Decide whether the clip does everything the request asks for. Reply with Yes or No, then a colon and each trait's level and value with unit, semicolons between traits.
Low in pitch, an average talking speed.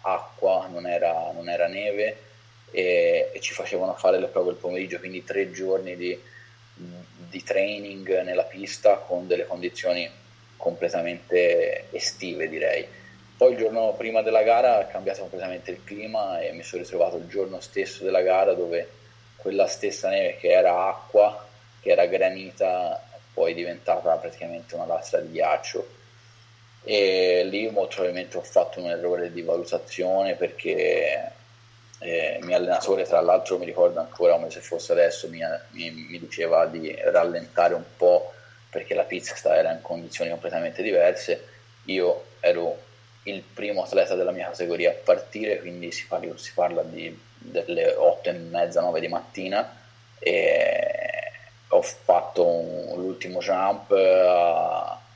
Yes: low, 115 Hz; average, 150 wpm